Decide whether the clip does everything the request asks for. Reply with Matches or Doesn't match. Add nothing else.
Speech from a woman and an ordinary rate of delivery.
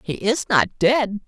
Doesn't match